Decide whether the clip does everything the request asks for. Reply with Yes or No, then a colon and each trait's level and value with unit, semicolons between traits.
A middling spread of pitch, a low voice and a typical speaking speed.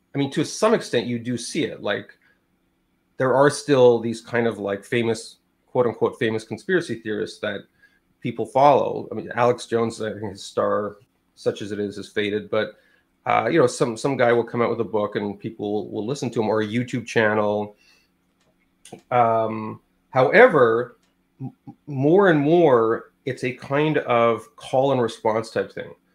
Yes: average, 3.2 semitones; low, 115 Hz; average, 180 wpm